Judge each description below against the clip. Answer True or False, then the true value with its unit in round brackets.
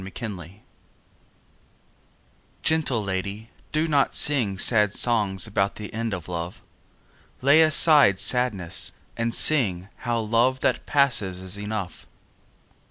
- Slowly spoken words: True (110 wpm)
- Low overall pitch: True (110 Hz)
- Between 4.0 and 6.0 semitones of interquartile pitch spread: True (4.8 semitones)